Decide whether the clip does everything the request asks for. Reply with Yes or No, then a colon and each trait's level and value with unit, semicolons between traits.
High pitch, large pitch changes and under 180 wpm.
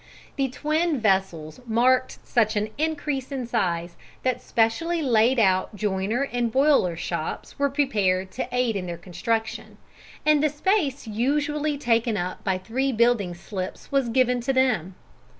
Yes: high, 235 Hz; wide, 6.0 semitones; average, 150 wpm